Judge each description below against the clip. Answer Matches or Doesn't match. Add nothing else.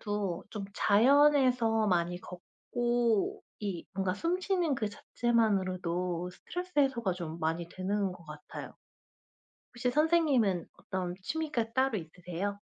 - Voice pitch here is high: Matches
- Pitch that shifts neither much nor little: Doesn't match